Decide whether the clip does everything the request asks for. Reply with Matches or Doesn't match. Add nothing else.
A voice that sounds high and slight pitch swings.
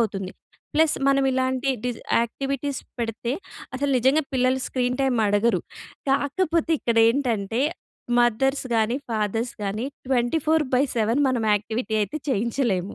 Doesn't match